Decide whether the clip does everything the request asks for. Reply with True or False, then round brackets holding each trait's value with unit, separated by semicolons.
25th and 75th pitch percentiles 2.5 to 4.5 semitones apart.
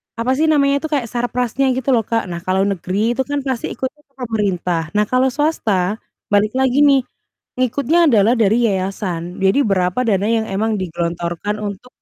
False (5.3 semitones)